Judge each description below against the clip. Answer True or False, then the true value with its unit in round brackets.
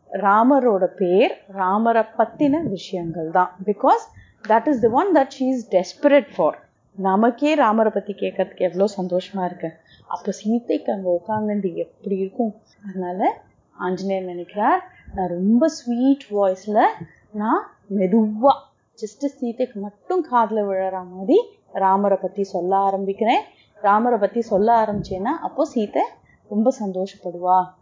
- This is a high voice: True (205 Hz)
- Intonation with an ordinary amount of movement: True (4.3 semitones)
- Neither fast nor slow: True (120 wpm)